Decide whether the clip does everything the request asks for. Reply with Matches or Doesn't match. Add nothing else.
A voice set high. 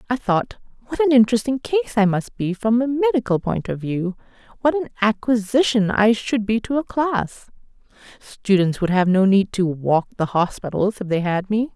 Matches